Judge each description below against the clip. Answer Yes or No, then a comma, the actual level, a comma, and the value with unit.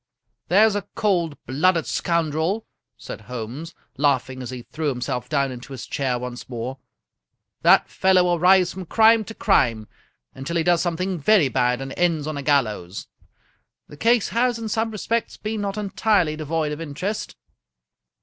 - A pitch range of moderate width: No, wide, 6.7 semitones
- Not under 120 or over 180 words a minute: Yes, average, 165 wpm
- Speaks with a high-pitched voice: No, medium, 160 Hz